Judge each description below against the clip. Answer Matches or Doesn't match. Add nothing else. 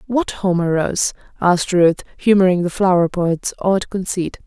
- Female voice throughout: Matches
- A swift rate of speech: Doesn't match